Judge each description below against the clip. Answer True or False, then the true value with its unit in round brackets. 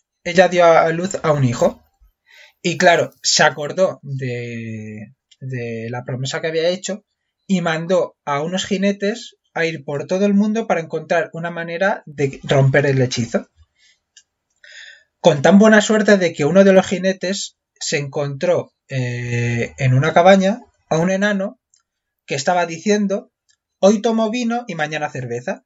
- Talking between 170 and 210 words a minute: False (150 wpm)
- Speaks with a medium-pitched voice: True (170 Hz)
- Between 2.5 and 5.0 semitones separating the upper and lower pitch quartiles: False (5.5 semitones)